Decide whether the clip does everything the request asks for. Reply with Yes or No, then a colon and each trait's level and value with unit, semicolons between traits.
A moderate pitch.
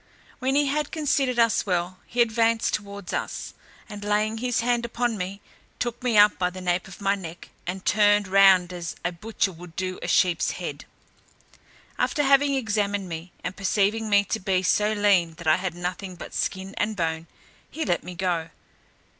No: high, 200 Hz